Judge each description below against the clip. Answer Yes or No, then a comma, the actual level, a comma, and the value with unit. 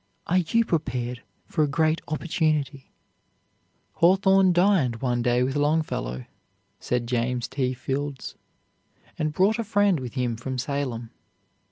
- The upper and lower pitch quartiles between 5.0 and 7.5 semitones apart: Yes, average, 5.3 semitones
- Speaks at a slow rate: Yes, slow, 130 wpm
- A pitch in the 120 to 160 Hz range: Yes, medium, 140 Hz